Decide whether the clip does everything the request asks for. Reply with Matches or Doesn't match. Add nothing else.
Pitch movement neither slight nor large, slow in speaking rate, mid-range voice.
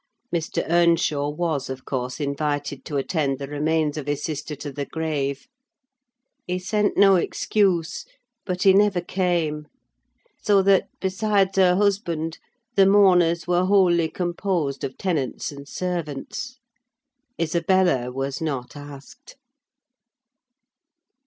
Matches